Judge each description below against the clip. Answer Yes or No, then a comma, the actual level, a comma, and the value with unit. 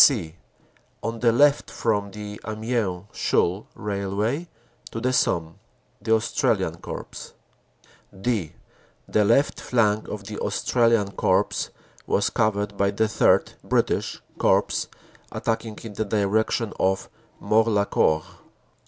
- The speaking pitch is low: Yes, low, 105 Hz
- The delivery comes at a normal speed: No, slow, 120 wpm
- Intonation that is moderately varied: No, narrow, 2.3 semitones